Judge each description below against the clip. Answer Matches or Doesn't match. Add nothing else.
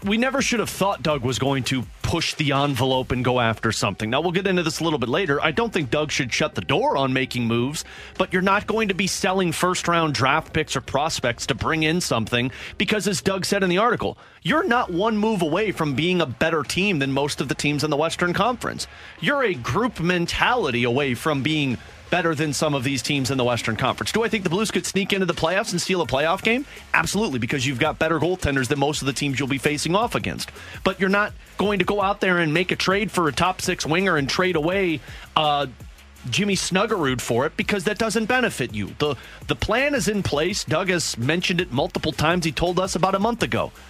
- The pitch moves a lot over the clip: Matches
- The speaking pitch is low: Doesn't match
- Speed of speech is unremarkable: Doesn't match